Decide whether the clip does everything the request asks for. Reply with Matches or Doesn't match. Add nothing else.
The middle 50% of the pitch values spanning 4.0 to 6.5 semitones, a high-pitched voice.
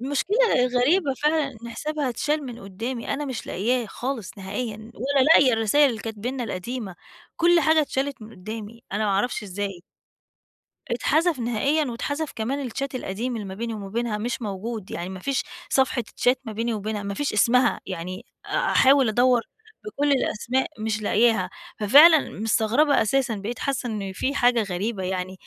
Matches